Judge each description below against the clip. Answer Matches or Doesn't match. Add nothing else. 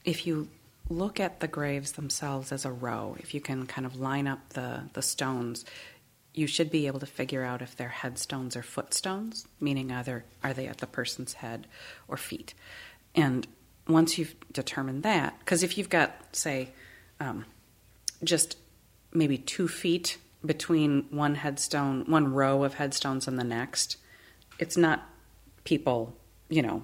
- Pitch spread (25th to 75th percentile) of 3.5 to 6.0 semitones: Matches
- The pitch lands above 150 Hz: Doesn't match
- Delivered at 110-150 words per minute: Doesn't match